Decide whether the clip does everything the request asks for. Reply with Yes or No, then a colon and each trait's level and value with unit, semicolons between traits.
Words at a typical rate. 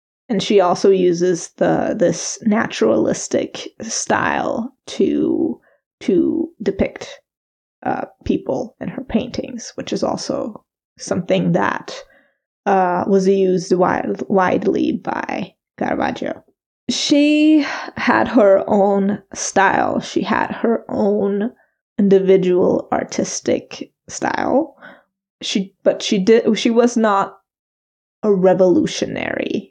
No: slow, 100 wpm